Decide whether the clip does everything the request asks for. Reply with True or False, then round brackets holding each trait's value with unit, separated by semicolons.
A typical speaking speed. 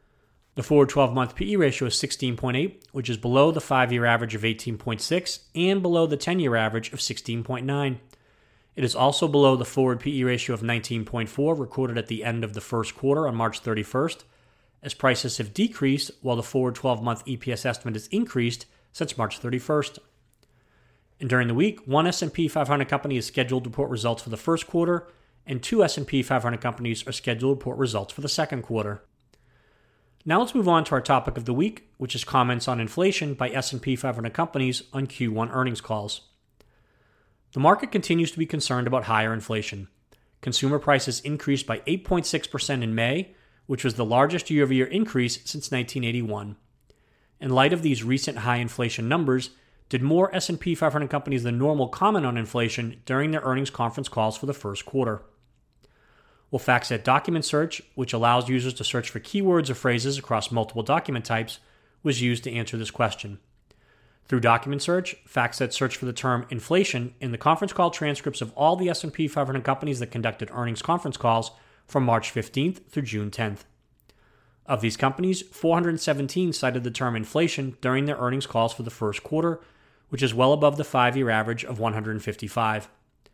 True (175 wpm)